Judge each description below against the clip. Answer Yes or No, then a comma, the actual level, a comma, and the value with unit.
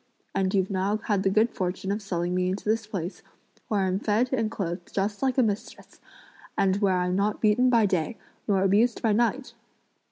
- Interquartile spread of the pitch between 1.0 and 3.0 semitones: Yes, average, 2.7 semitones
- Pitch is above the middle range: Yes, high, 200 Hz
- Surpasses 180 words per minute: Yes, average, 195 wpm